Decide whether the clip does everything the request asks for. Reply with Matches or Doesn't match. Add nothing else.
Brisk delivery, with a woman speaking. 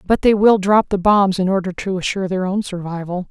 Matches